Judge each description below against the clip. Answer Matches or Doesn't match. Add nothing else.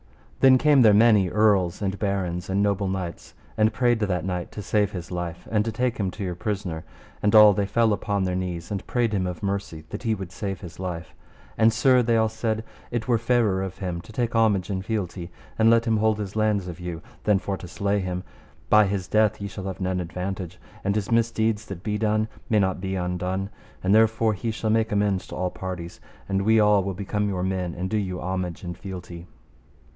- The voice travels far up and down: Doesn't match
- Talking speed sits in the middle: Doesn't match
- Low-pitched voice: Matches